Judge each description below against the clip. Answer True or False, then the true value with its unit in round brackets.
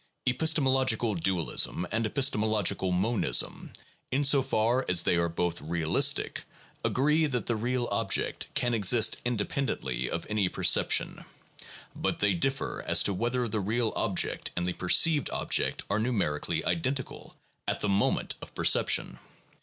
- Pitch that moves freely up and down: True (5.7 semitones)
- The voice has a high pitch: False (110 Hz)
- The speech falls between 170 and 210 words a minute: False (140 wpm)